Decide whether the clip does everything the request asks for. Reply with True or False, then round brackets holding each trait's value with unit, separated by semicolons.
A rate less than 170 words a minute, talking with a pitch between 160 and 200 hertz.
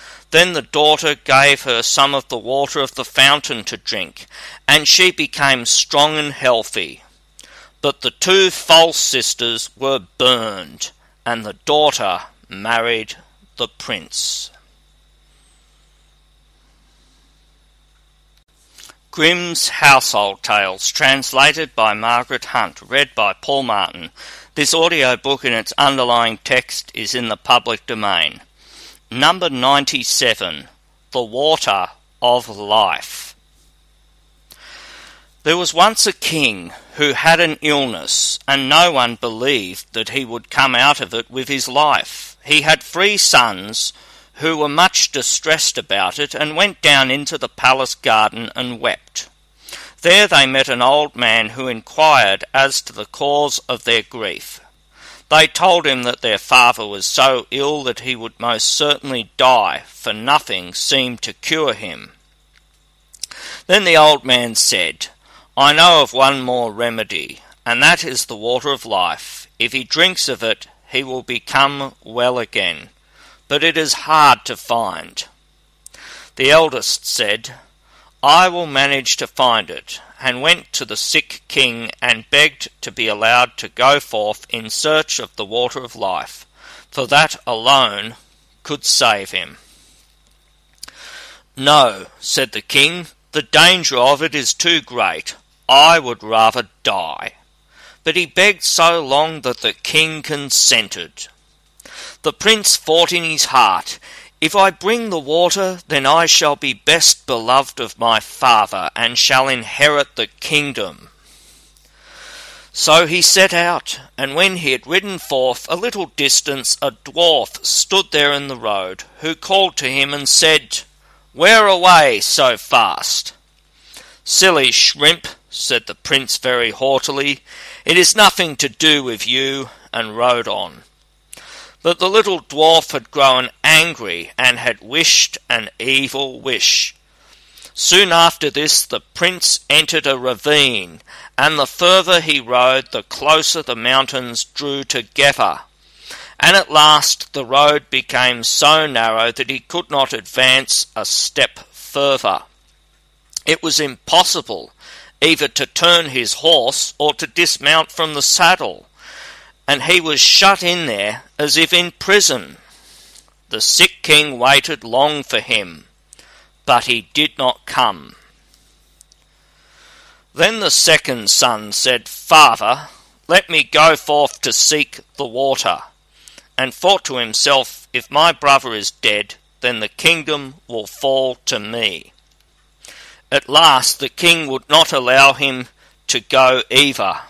False (140 wpm; 140 Hz)